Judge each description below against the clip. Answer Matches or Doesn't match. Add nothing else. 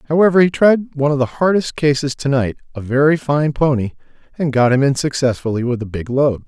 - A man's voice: Matches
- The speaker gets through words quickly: Matches